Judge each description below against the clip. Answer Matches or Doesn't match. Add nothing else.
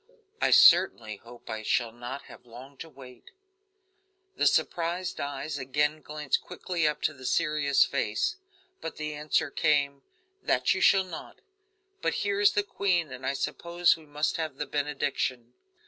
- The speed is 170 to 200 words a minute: Doesn't match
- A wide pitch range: Doesn't match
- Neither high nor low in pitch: Matches